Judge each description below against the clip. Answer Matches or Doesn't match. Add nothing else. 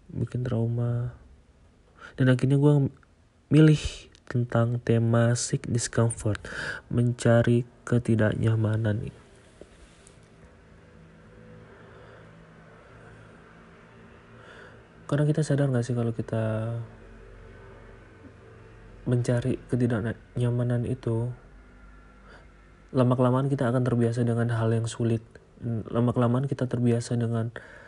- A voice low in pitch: Matches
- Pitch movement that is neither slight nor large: Doesn't match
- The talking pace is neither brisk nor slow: Doesn't match